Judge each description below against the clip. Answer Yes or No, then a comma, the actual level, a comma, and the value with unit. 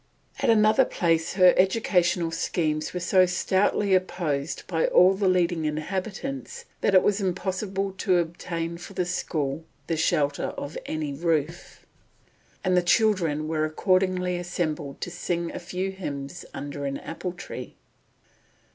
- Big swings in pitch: No, average, 2.9 semitones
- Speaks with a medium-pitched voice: Yes, medium, 175 Hz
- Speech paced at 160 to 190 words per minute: No, average, 140 wpm